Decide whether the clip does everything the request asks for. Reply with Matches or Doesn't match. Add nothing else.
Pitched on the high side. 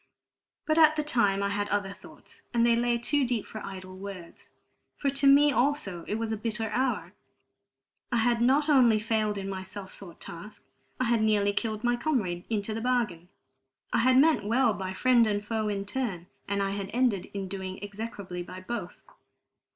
Matches